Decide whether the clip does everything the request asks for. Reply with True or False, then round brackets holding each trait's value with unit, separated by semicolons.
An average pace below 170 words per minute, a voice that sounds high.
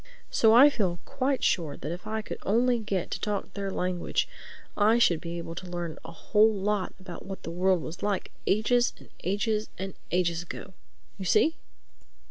False (185 wpm; 195 Hz)